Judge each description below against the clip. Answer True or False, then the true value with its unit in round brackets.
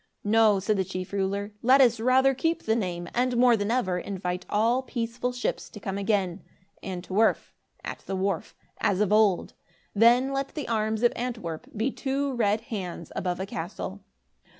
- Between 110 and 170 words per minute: False (180 wpm)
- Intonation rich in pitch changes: False (4.2 semitones)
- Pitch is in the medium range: False (215 Hz)